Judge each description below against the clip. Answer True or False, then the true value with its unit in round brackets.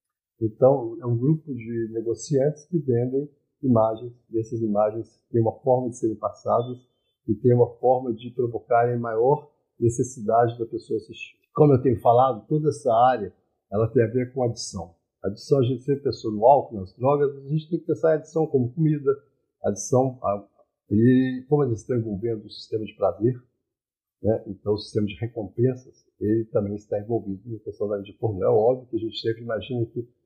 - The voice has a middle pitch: False (120 Hz)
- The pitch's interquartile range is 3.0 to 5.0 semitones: True (3.6 semitones)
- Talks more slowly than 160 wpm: False (180 wpm)